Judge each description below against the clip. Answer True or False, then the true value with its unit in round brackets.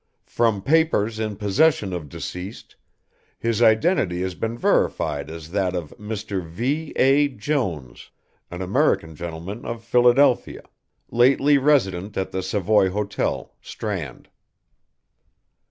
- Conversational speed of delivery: False (115 wpm)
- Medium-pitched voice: False (105 Hz)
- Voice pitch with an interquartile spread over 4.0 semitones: True (5.2 semitones)